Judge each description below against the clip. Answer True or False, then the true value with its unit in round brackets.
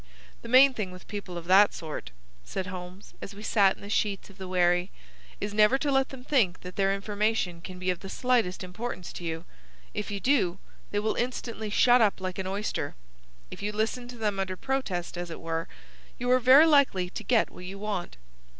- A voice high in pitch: True (200 Hz)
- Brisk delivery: True (215 wpm)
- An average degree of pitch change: True (4.2 semitones)